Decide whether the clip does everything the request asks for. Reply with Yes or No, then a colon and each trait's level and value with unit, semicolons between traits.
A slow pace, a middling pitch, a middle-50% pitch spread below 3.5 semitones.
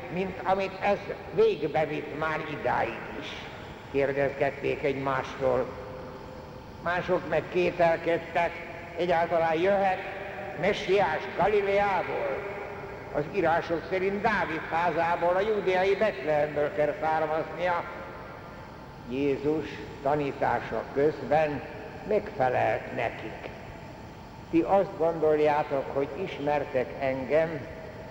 No: slow, 80 wpm; medium, 165 Hz; average, 4.1 semitones